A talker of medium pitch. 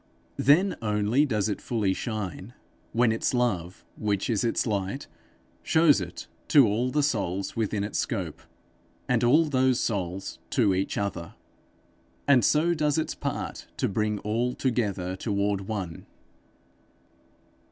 No: low, 110 Hz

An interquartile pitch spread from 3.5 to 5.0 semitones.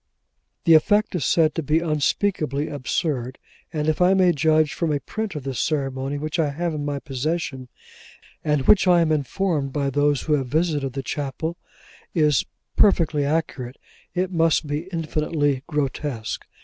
No: average, 2.9 semitones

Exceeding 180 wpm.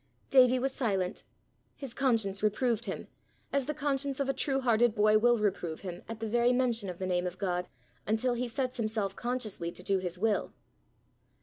Yes: average, 190 wpm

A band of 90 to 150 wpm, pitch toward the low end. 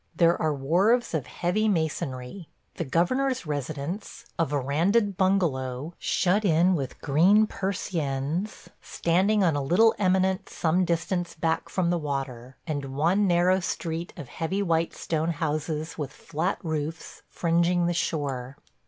No: slow, 135 wpm; medium, 165 Hz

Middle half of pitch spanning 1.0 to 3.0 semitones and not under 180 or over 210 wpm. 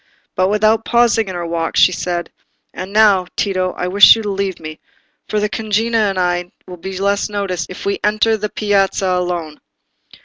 Yes: average, 2.7 semitones; average, 190 wpm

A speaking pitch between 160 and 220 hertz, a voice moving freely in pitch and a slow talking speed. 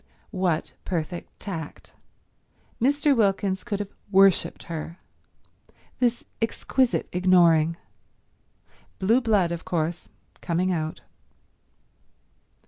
No: medium, 185 Hz; average, 4.0 semitones; slow, 85 wpm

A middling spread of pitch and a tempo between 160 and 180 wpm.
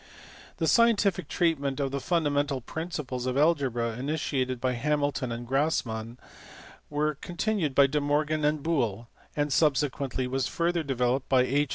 No: average, 3.1 semitones; average, 150 wpm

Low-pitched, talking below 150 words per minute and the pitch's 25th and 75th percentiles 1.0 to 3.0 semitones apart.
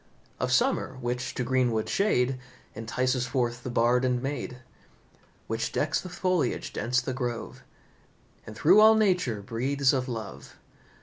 Yes: low, 125 Hz; average, 140 wpm; narrow, 2.4 semitones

